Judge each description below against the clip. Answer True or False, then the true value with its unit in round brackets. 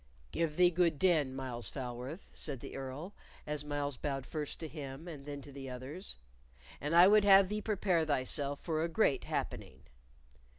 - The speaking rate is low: False (175 wpm)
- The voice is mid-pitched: True (150 Hz)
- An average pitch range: True (4.1 semitones)